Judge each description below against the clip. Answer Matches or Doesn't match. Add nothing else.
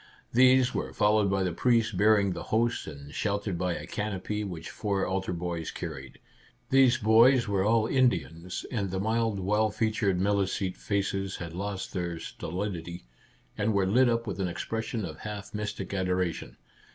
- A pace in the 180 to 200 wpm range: Doesn't match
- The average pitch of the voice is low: Matches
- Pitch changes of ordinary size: Matches